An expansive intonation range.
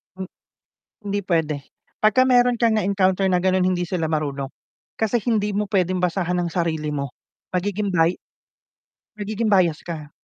No: average, 3.7 semitones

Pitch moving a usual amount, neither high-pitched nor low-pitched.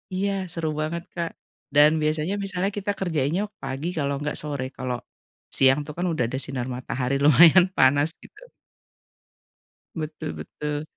Yes: average, 3.5 semitones; medium, 150 Hz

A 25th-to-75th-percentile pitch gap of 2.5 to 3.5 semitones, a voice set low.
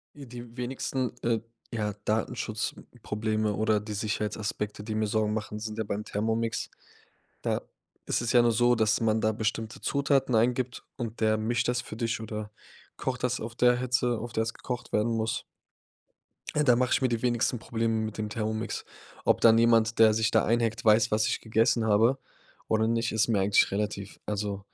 No: narrow, 1.9 semitones; low, 110 Hz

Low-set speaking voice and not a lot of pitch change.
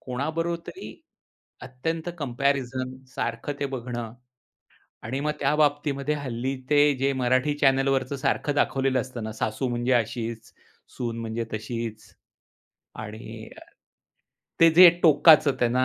No: low, 130 Hz; average, 3.5 semitones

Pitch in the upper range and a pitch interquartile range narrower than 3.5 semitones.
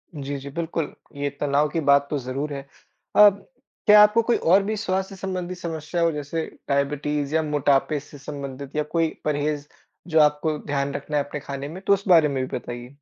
No: medium, 150 Hz; average, 2.9 semitones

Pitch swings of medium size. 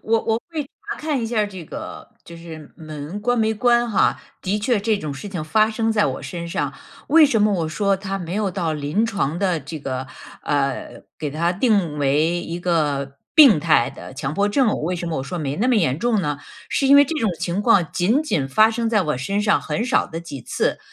No: wide, 6.2 semitones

